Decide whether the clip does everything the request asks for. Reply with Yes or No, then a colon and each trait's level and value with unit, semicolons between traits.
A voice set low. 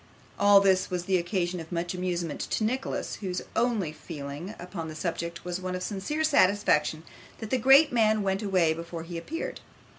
No: medium, 185 Hz